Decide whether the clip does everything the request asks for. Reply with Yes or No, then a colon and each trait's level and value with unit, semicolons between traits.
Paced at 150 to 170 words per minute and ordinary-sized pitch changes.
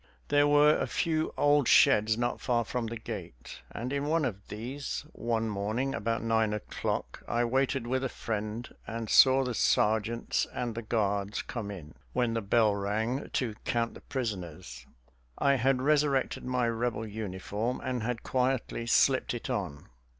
Yes: average, 165 wpm; average, 3.3 semitones